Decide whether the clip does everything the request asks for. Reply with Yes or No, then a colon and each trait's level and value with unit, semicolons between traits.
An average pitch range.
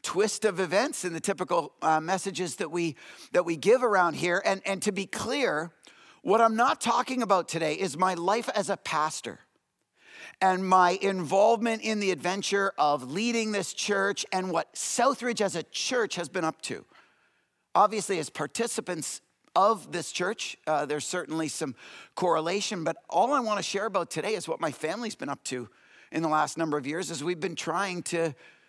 Yes: average, 4.1 semitones